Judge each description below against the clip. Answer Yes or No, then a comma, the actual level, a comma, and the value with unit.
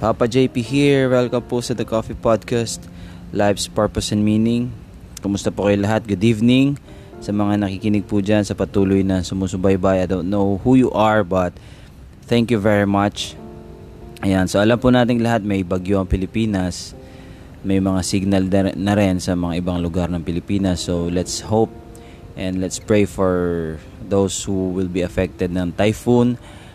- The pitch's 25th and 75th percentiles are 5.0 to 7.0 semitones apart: No, average, 3.2 semitones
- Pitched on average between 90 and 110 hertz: Yes, low, 100 Hz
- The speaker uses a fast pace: No, average, 165 wpm